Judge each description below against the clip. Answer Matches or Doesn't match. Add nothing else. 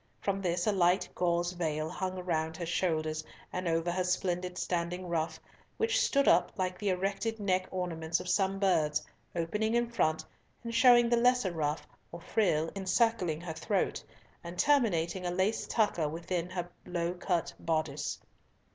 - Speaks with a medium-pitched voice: Matches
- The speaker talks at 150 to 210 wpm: Matches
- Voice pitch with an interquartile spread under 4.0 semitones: Matches